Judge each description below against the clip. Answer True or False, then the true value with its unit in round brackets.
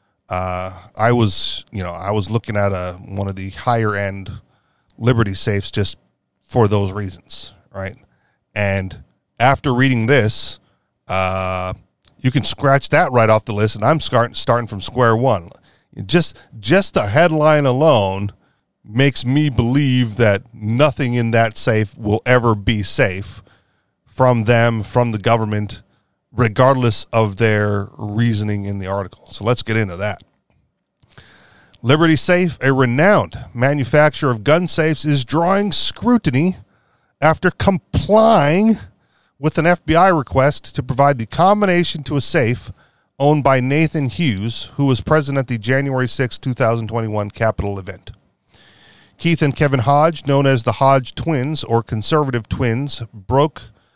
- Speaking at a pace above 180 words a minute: False (145 wpm)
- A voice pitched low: True (120 Hz)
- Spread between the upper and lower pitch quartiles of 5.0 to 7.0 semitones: True (5.5 semitones)